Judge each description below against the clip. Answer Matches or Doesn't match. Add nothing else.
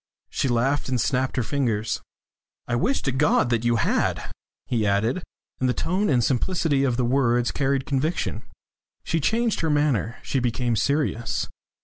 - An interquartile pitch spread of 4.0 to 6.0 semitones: Doesn't match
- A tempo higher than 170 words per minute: Doesn't match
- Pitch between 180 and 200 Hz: Doesn't match